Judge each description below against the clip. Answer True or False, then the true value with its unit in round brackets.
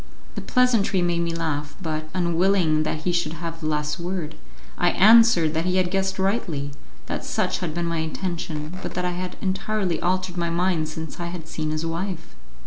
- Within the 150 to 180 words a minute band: False (195 wpm)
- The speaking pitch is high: False (170 Hz)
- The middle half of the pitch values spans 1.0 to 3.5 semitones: True (2.8 semitones)